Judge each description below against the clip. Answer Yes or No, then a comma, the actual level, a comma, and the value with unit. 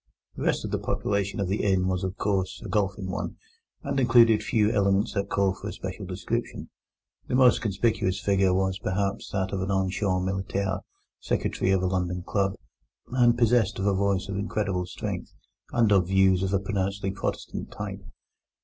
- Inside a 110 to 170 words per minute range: No, average, 180 wpm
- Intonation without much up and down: Yes, narrow, 1.5 semitones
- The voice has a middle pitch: No, low, 100 Hz